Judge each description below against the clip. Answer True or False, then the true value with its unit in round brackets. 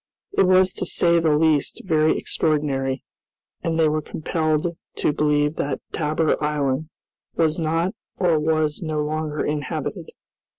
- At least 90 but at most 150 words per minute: True (135 wpm)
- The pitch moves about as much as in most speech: False (1.5 semitones)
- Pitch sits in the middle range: True (155 Hz)